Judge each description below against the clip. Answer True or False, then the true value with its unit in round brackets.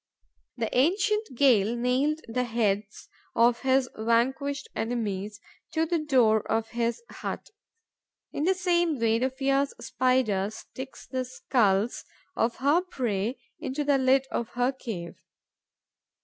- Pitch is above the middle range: True (250 Hz)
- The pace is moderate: False (130 wpm)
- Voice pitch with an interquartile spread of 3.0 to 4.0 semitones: True (3.7 semitones)